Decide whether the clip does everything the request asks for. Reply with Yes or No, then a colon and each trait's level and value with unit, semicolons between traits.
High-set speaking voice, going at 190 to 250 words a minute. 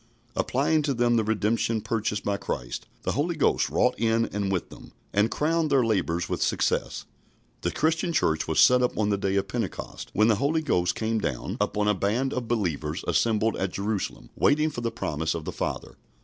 No: low, 110 Hz; average, 200 wpm